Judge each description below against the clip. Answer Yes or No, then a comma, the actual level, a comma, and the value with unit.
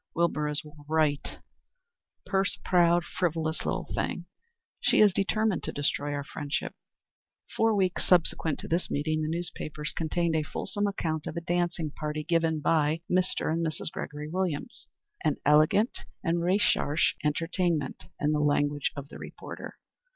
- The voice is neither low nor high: Yes, medium, 160 Hz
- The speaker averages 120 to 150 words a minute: Yes, average, 145 wpm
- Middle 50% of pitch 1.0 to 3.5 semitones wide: Yes, average, 2.8 semitones